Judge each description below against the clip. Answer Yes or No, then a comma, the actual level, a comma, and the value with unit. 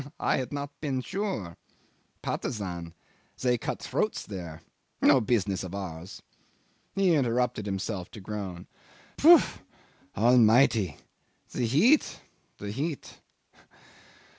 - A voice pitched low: Yes, low, 110 Hz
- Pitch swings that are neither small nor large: No, wide, 6.2 semitones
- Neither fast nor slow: No, slow, 105 wpm